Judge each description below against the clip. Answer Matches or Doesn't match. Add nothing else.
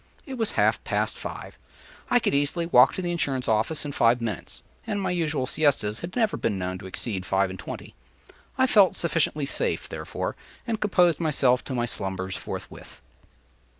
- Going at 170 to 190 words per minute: Matches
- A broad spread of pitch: Matches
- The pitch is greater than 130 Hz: Matches